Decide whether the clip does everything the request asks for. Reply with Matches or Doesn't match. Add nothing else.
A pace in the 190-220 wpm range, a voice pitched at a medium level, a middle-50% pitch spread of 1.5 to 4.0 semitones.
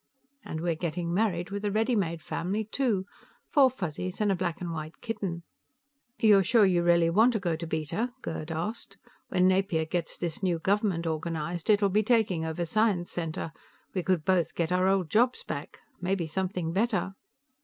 Doesn't match